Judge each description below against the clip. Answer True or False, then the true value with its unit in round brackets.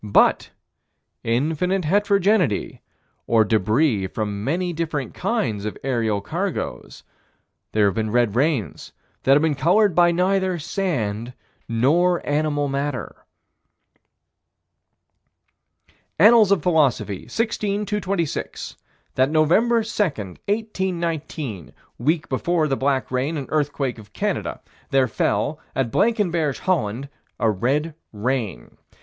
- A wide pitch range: True (7.3 semitones)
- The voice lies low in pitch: False (145 Hz)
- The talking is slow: True (110 wpm)